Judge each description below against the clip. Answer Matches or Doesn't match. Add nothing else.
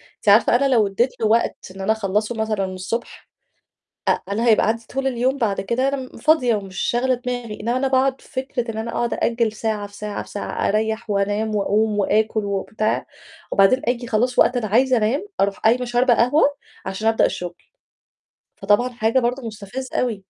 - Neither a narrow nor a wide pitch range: Matches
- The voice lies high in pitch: Matches